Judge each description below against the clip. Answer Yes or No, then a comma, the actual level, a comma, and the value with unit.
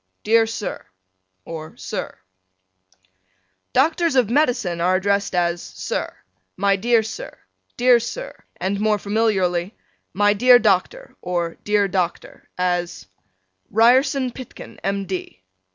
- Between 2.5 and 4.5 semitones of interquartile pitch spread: No, average, 4.9 semitones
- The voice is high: Yes, high, 205 Hz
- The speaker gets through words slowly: Yes, slow, 115 wpm